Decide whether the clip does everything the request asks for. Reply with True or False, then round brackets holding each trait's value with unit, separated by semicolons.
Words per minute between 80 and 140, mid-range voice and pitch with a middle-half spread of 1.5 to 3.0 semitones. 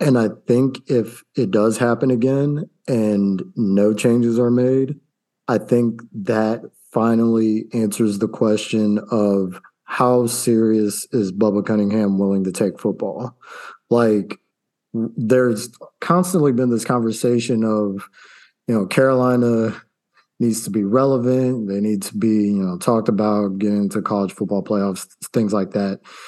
False (135 wpm; 110 Hz; 2.7 semitones)